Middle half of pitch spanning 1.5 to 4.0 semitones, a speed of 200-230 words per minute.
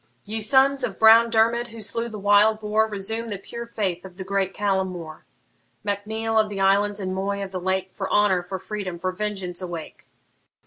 Yes: narrow, 2.6 semitones; fast, 205 wpm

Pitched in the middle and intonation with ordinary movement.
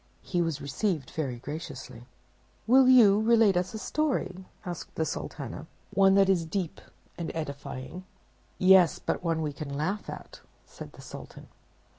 Yes: medium, 175 Hz; average, 4.6 semitones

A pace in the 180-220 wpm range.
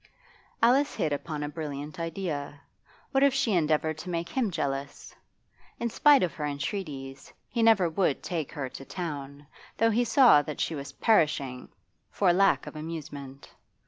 No: average, 160 wpm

